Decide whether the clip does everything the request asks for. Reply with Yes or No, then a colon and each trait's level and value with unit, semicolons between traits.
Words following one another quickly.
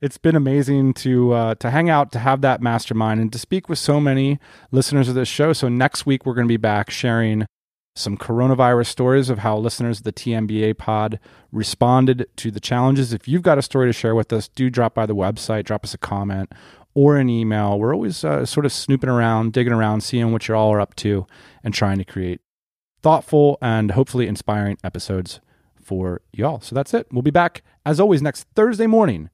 Yes: fast, 210 wpm